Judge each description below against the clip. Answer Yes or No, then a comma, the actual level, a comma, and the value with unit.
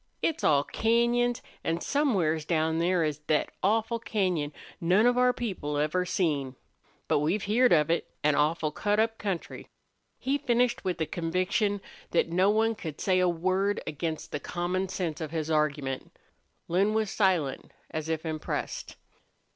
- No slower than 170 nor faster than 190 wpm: No, average, 160 wpm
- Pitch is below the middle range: No, medium, 180 Hz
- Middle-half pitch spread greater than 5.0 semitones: Yes, wide, 5.4 semitones